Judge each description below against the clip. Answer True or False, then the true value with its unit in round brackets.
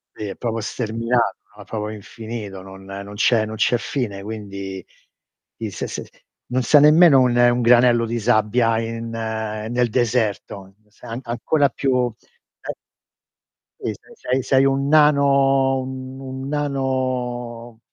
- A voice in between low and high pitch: False (120 Hz)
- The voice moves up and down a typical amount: True (3.2 semitones)